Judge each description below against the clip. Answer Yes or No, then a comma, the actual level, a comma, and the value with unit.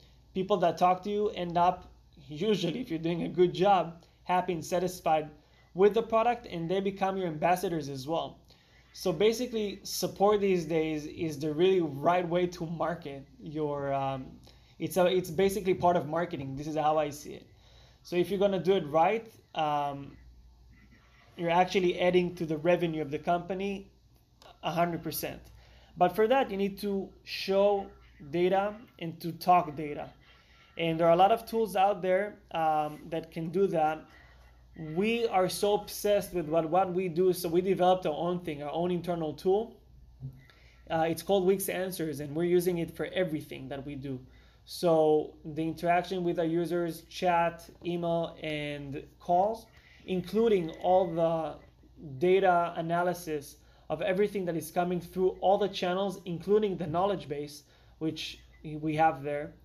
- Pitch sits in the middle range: Yes, medium, 175 Hz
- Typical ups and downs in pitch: Yes, average, 3.1 semitones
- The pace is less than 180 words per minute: Yes, average, 165 wpm